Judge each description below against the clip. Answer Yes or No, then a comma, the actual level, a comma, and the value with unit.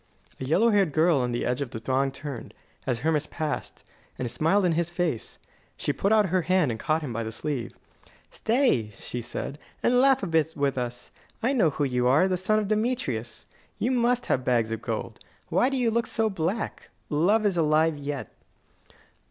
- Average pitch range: No, wide, 8.0 semitones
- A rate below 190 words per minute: No, average, 200 wpm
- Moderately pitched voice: Yes, medium, 155 Hz